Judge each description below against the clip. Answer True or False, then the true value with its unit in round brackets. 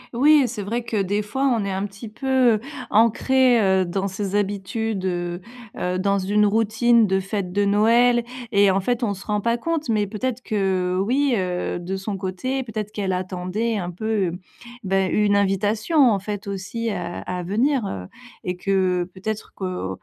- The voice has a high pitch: True (205 Hz)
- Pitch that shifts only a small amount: False (3.3 semitones)